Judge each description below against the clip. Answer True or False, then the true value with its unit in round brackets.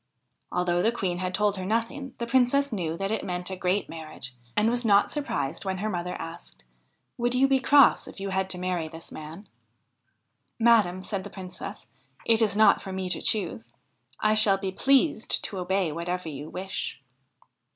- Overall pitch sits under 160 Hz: False (190 Hz)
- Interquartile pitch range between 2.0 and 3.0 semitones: False (3.9 semitones)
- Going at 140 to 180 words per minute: False (200 wpm)